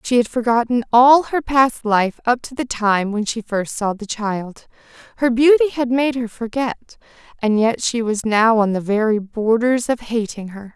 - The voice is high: Yes, high, 230 Hz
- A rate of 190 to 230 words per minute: Yes, average, 195 wpm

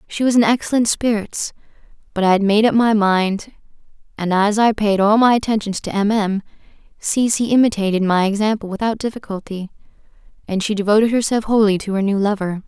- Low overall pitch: No, high, 210 Hz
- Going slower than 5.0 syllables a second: No, 5.8 syllables/s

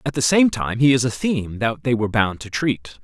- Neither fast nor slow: No, fast, 275 wpm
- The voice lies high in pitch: No, low, 120 Hz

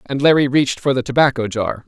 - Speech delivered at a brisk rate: Yes, fast, 225 wpm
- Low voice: Yes, low, 130 Hz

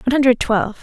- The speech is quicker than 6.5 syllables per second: Yes, 8.5 syllables/s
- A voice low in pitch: No, high, 235 Hz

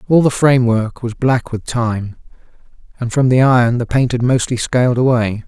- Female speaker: No, male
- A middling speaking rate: Yes, average, 185 wpm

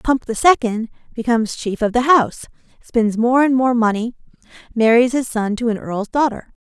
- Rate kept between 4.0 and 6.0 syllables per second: Yes, 5.1 syllables/s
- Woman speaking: Yes, female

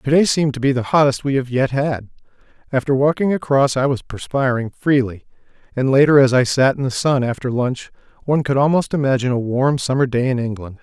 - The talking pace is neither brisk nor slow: No, fast, 210 wpm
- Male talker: Yes, male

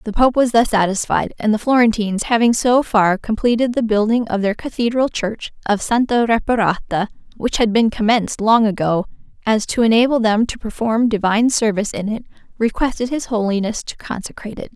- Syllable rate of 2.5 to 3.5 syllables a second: No, 5.6 syllables/s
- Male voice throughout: No, female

